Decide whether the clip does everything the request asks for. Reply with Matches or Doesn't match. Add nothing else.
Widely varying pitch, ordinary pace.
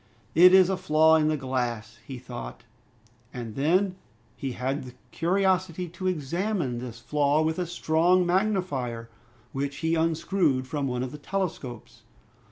Matches